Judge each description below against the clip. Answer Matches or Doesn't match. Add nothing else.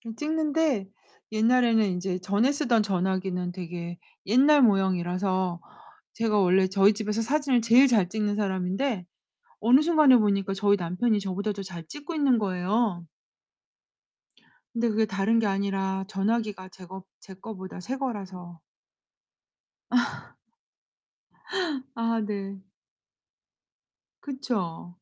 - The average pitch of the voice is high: Matches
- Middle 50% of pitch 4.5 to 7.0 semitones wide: Doesn't match